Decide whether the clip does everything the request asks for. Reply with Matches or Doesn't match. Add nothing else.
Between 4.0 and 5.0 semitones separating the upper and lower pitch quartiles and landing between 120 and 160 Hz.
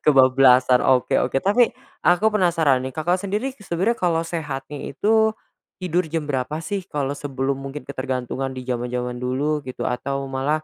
Matches